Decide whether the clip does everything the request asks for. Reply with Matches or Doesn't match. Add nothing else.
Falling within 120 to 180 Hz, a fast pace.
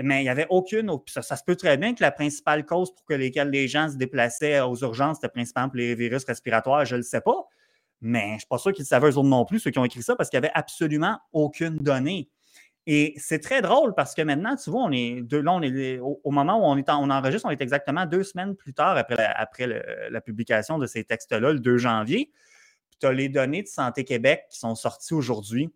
Matches